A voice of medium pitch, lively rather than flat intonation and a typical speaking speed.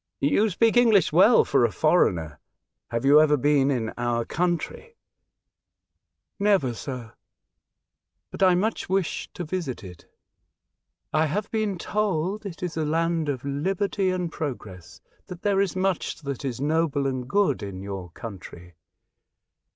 Yes: medium, 155 Hz; wide, 7.4 semitones; average, 150 wpm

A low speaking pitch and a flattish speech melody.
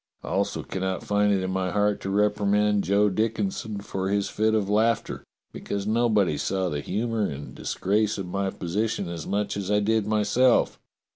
Yes: low, 105 Hz; narrow, 2.0 semitones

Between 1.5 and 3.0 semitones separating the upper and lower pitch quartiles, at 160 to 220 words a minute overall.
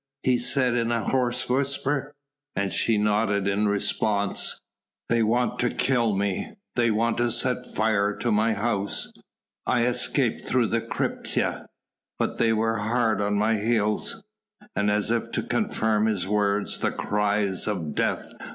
No: narrow, 2.6 semitones; average, 150 wpm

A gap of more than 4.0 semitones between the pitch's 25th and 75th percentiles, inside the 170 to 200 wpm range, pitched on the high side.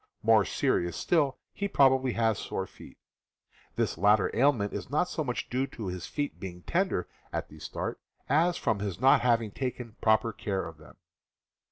No: average, 5.3 semitones; average, 175 wpm; low, 115 Hz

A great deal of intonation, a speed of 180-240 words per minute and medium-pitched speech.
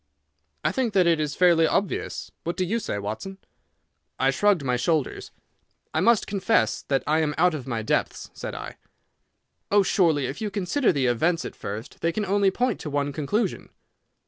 Yes: wide, 6.0 semitones; average, 185 wpm; medium, 165 Hz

